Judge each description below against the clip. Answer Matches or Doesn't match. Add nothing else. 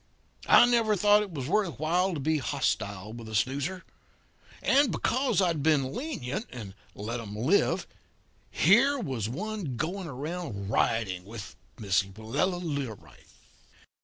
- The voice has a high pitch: Doesn't match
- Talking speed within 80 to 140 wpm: Matches